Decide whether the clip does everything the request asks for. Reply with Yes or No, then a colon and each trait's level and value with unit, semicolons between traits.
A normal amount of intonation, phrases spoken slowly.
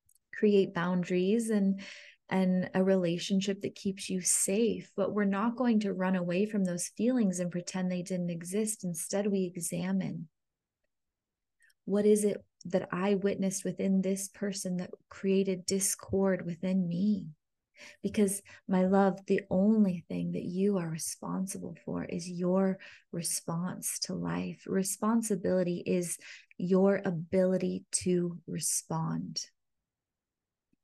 No: narrow, 1.8 semitones; slow, 125 wpm